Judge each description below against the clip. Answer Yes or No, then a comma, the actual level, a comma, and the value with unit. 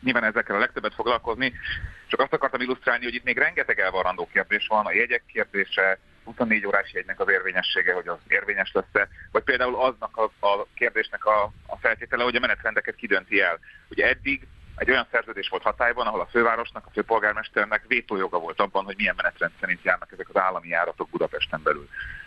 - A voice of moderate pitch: No, low, 110 Hz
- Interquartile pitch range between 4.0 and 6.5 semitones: Yes, average, 4.5 semitones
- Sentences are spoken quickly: Yes, fast, 180 wpm